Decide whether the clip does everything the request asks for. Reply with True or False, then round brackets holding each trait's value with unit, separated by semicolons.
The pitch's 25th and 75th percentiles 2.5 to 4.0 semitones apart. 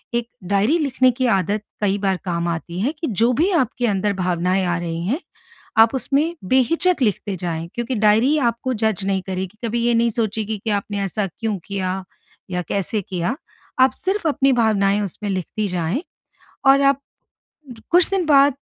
False (5.3 semitones)